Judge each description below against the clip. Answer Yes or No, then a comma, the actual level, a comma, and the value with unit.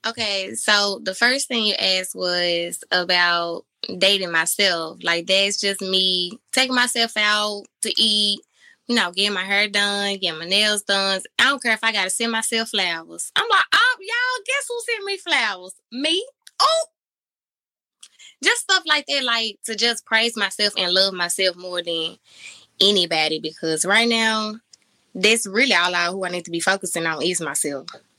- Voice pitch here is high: Yes, high, 200 Hz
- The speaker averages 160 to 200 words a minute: Yes, average, 170 wpm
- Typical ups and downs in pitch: Yes, average, 4.3 semitones